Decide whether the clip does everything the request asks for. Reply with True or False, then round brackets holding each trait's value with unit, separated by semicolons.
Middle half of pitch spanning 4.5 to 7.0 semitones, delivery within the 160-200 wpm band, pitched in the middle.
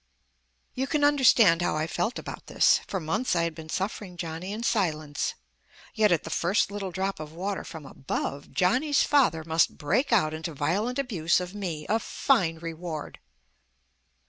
True (5.1 semitones; 170 wpm; 180 Hz)